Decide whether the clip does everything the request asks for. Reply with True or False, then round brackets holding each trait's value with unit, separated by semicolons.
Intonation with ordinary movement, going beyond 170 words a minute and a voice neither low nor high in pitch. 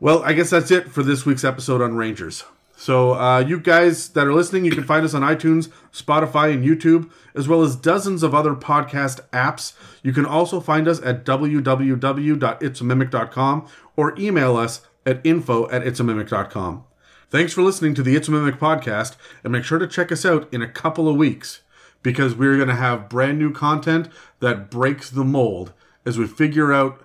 True (3.9 semitones; 190 wpm; 145 Hz)